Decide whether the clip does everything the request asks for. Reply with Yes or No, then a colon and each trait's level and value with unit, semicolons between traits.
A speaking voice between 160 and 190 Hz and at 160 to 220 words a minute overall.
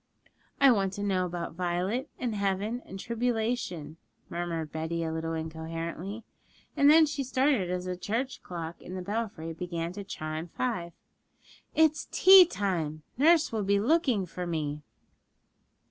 No: medium, 185 Hz; average, 145 wpm